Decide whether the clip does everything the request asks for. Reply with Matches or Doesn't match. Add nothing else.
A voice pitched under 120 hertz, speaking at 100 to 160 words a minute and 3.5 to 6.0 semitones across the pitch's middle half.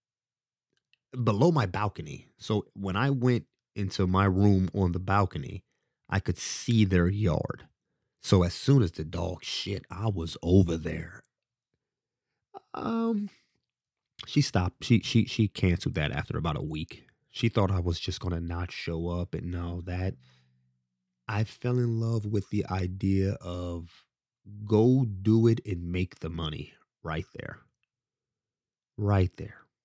Matches